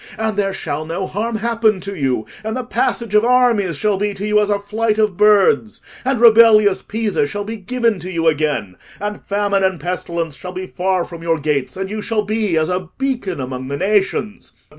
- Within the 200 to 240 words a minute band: Yes, fast, 205 wpm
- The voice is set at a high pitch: Yes, high, 200 Hz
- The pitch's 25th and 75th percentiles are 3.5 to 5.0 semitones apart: Yes, average, 3.8 semitones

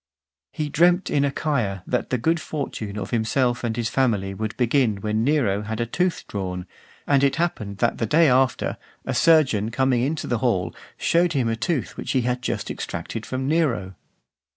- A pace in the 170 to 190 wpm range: Yes, average, 185 wpm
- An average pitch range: Yes, average, 4.7 semitones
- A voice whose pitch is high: No, low, 125 Hz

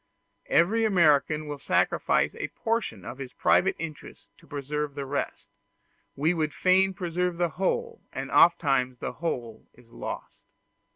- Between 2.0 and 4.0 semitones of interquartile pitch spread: No, average, 4.5 semitones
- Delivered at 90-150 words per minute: Yes, average, 140 wpm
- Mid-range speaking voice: Yes, medium, 155 Hz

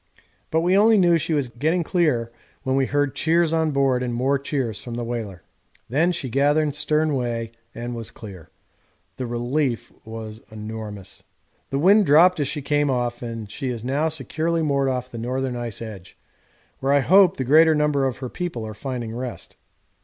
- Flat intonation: No, average, 4.6 semitones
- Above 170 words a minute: Yes, average, 185 wpm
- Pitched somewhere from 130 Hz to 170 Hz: Yes, low, 135 Hz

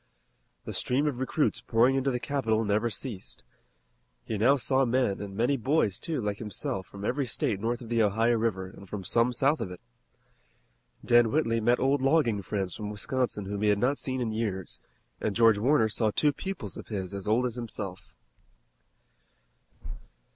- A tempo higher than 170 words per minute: Yes, average, 180 wpm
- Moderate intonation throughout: Yes, average, 4.0 semitones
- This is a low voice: Yes, low, 115 Hz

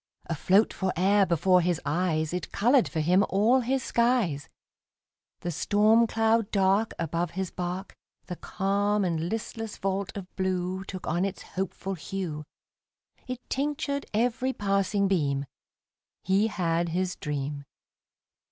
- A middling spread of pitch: Yes, average, 3.5 semitones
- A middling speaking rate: No, slow, 130 wpm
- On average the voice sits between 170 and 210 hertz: Yes, high, 190 Hz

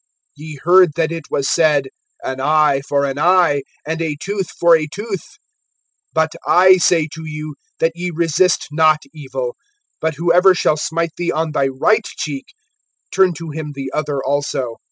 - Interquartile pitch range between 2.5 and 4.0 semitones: Yes, average, 2.9 semitones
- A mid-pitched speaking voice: Yes, medium, 160 Hz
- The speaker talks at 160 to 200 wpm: Yes, average, 170 wpm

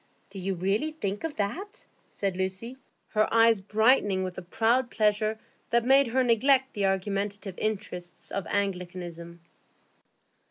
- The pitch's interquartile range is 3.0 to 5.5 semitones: Yes, average, 3.6 semitones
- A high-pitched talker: Yes, high, 205 Hz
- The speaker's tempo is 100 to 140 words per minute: Yes, slow, 135 wpm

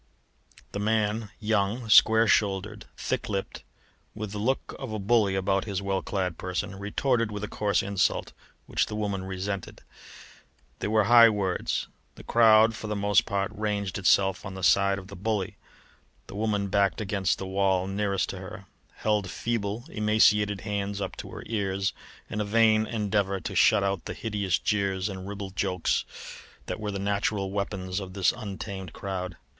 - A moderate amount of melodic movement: No, narrow, 1.7 semitones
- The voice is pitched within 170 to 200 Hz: No, low, 100 Hz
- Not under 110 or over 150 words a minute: No, average, 170 wpm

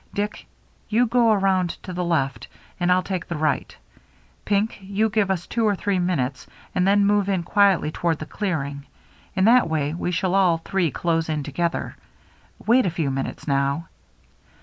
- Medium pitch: Yes, medium, 180 Hz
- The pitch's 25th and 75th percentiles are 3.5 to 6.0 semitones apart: Yes, average, 4.1 semitones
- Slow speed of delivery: No, average, 175 wpm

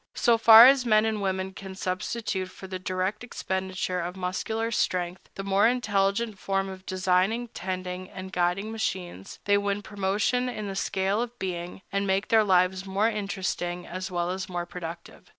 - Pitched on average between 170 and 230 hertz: Yes, high, 190 Hz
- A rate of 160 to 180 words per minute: Yes, average, 170 wpm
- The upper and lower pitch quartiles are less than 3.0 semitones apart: Yes, narrow, 2.5 semitones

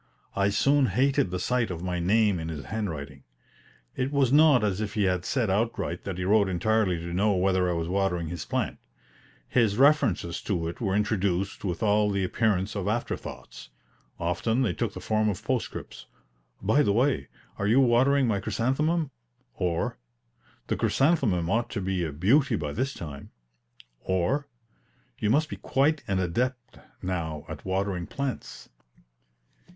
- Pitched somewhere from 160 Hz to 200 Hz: No, low, 100 Hz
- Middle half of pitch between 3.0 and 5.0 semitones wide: No, wide, 5.4 semitones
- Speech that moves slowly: No, average, 165 wpm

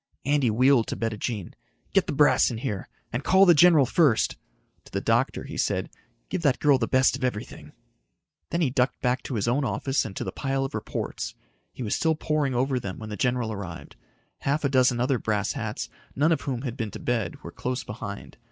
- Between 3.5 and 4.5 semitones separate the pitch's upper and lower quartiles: Yes, average, 3.9 semitones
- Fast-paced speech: Yes, fast, 215 wpm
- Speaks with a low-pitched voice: Yes, low, 125 Hz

